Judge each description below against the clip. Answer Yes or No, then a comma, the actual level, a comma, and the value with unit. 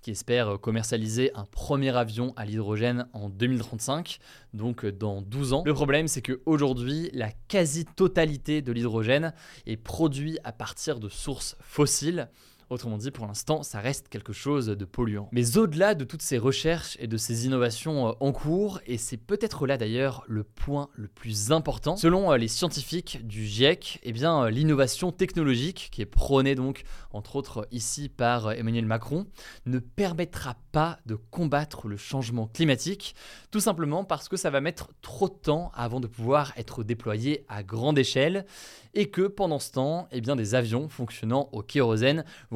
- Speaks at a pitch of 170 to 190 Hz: No, low, 135 Hz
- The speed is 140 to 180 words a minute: Yes, average, 170 wpm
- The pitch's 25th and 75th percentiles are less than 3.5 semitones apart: No, average, 5.1 semitones